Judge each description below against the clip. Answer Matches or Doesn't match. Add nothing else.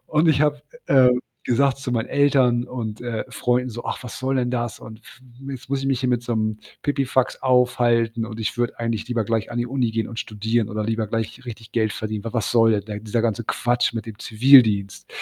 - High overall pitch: Doesn't match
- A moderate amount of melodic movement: Doesn't match